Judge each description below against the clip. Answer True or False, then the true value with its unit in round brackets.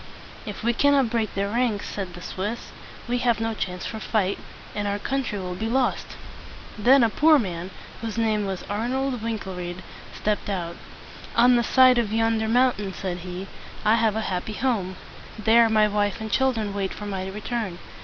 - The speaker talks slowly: False (195 wpm)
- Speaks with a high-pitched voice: True (215 Hz)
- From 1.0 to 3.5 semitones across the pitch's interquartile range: True (3.2 semitones)